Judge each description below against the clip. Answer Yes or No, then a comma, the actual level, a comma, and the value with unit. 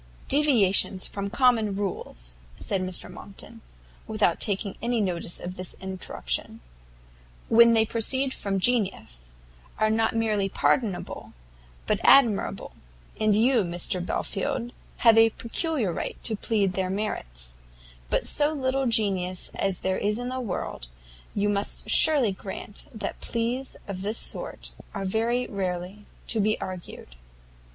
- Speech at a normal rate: No, slow, 130 wpm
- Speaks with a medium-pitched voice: No, high, 210 Hz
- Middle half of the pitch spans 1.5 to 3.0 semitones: No, average, 3.7 semitones